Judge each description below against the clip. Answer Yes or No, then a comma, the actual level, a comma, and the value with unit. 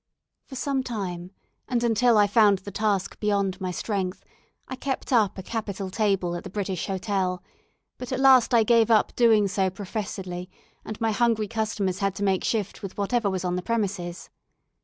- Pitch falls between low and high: No, high, 205 Hz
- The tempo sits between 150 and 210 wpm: Yes, average, 180 wpm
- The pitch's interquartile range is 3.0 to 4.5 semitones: Yes, average, 3.3 semitones